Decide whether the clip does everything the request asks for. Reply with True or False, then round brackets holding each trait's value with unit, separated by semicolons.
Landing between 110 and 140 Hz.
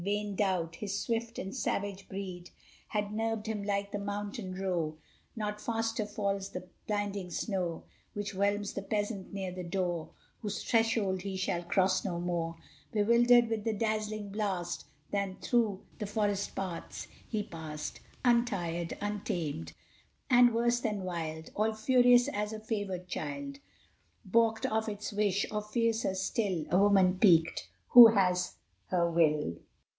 False (200 Hz)